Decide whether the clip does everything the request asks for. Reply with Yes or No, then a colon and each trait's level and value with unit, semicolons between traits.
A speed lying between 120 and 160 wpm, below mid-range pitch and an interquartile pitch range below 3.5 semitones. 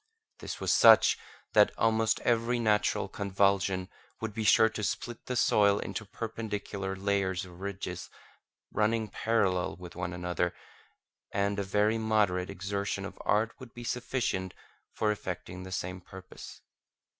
Yes: average, 140 wpm; low, 100 Hz; average, 2.9 semitones